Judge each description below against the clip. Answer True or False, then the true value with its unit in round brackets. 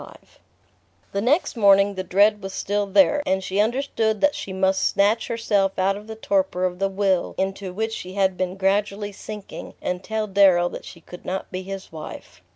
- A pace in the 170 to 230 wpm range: True (195 wpm)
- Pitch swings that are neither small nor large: False (1.9 semitones)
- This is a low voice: False (195 Hz)